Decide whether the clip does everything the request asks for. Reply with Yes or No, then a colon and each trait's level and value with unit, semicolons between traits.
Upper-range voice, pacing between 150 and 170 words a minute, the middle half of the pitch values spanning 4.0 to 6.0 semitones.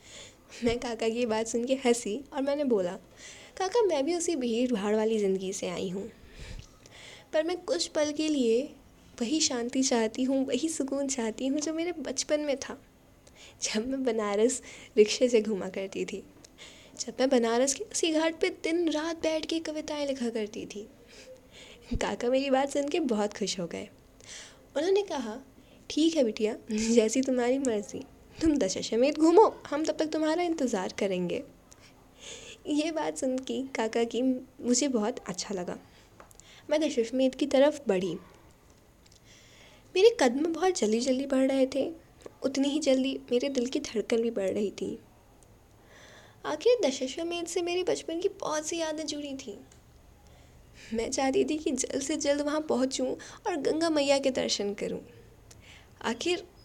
Yes: very high, 265 Hz; average, 160 wpm; average, 5.3 semitones